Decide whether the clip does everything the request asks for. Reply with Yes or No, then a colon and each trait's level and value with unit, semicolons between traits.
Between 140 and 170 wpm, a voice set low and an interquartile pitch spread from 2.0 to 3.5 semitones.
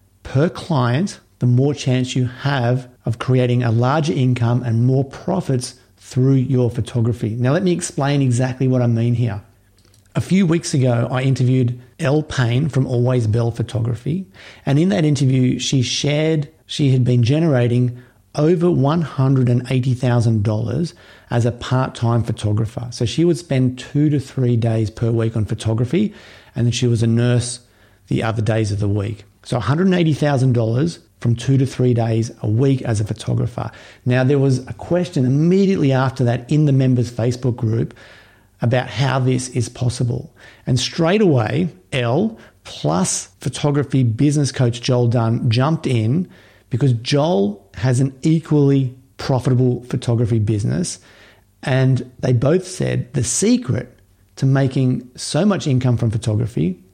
Yes: average, 150 wpm; low, 125 Hz; average, 2.8 semitones